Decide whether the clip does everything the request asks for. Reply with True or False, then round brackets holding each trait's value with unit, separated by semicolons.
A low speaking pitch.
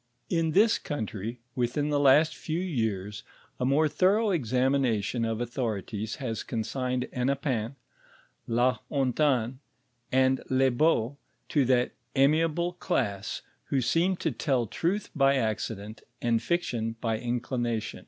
True (130 Hz)